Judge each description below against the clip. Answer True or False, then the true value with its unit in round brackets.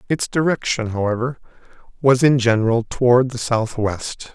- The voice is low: True (120 Hz)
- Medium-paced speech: False (125 wpm)